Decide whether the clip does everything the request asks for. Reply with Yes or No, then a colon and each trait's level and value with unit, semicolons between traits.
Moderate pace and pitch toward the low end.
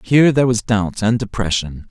Yes: average, 190 wpm; low, 110 Hz